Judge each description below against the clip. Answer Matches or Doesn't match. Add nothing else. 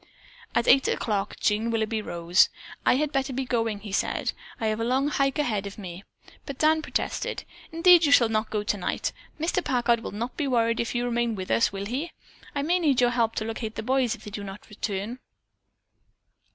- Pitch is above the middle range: Matches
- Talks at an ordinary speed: Doesn't match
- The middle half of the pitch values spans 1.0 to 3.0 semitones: Doesn't match